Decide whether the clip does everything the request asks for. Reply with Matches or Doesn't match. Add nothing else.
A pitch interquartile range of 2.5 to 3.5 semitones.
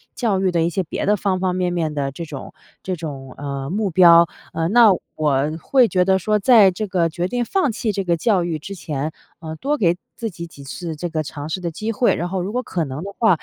Doesn't match